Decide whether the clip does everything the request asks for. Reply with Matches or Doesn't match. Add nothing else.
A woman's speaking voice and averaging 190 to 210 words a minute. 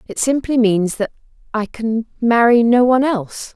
Doesn't match